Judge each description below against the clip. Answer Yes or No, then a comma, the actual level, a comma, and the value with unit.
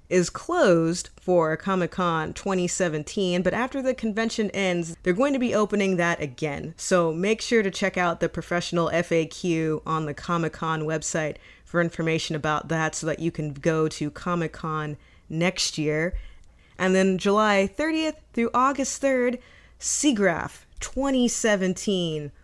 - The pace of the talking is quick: No, average, 145 wpm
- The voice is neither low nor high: Yes, medium, 175 Hz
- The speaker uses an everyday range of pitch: Yes, average, 4.5 semitones